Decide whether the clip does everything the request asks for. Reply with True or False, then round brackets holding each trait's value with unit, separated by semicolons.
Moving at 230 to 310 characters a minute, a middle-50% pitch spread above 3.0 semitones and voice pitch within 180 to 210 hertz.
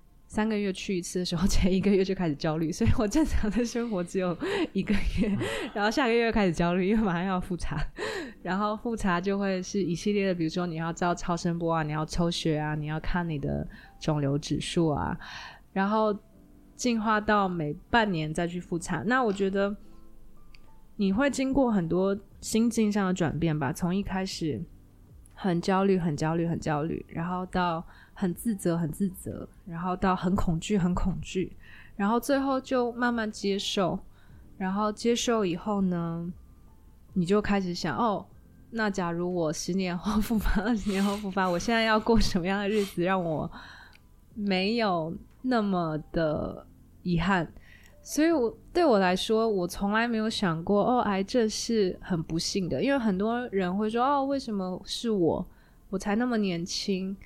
True (255 characters per minute; 3.9 semitones; 190 Hz)